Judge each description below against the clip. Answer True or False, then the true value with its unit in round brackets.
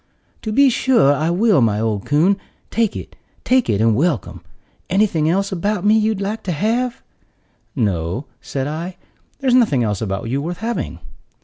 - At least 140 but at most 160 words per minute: False (170 wpm)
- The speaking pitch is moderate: True (175 Hz)